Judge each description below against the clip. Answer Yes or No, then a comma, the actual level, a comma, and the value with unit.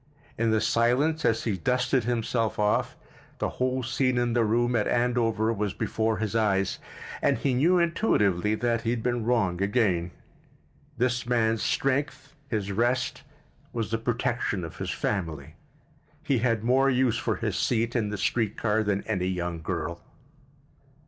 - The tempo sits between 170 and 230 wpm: No, average, 160 wpm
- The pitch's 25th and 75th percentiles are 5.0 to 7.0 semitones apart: No, average, 2.8 semitones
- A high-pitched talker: No, low, 115 Hz